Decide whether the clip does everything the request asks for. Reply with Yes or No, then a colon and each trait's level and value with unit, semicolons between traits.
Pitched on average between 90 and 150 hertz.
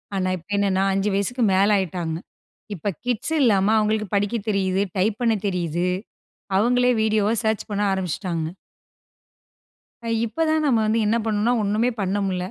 No: high, 205 Hz